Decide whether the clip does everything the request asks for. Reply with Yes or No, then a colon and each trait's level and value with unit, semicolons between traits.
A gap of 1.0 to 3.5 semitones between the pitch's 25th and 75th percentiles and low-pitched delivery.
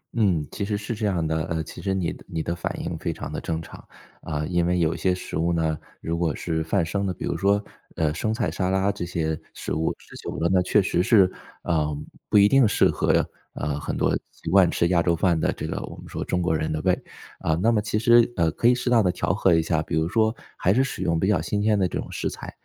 No: average, 3.9 semitones; very low, 90 Hz